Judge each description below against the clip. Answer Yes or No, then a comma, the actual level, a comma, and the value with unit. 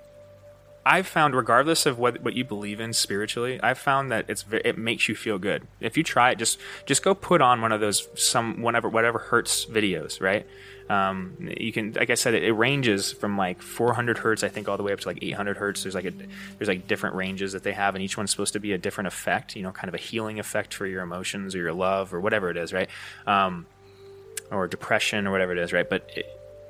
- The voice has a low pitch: Yes, low, 105 Hz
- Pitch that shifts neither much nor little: Yes, average, 3.6 semitones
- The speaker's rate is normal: No, fast, 240 wpm